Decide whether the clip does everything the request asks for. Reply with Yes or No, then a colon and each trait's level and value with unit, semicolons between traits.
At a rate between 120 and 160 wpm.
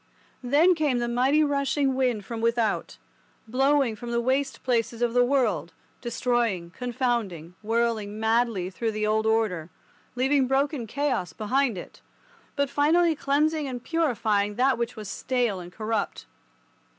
Yes: average, 140 wpm